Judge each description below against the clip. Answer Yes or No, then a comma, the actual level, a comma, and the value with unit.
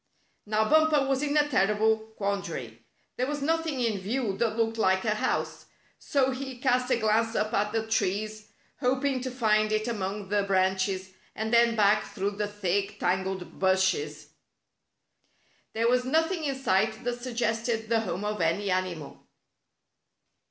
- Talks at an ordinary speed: Yes, average, 160 wpm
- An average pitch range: Yes, average, 4.0 semitones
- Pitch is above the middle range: Yes, high, 220 Hz